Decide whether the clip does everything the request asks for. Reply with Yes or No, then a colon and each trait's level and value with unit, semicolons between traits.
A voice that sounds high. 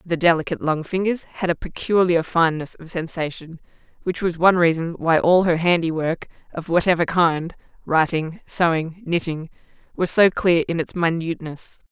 No: medium, 170 Hz